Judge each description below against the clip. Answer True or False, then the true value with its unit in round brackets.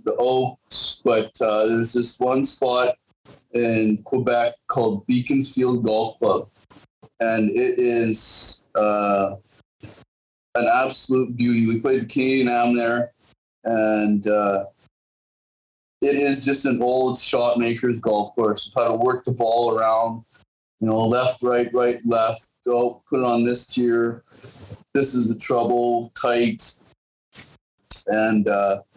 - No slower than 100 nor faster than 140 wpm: True (135 wpm)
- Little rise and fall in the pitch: True (2.1 semitones)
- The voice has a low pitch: True (120 Hz)